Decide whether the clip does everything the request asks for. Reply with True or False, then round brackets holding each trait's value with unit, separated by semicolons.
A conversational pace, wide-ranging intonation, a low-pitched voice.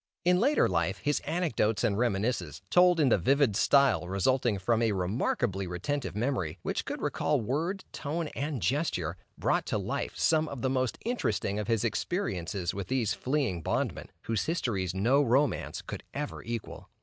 True (165 wpm; 6.9 semitones; 120 Hz)